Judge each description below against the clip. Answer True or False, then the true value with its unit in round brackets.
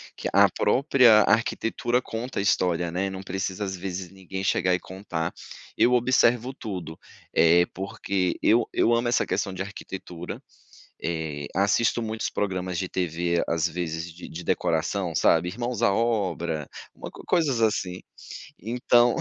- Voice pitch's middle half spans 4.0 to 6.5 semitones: True (4.6 semitones)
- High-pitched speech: False (95 Hz)